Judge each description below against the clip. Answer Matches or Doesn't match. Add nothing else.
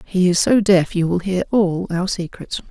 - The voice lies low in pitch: Doesn't match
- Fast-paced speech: Matches